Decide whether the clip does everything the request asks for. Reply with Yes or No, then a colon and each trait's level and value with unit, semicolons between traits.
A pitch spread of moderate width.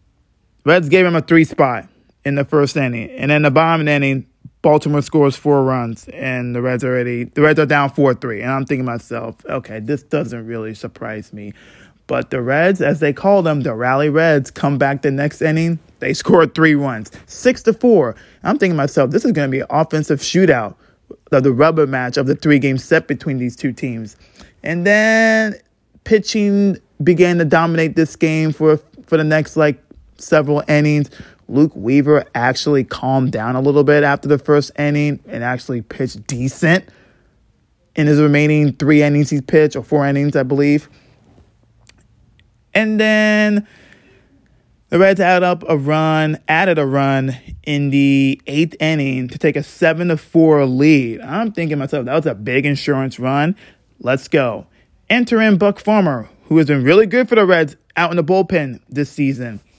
Yes: average, 3.5 semitones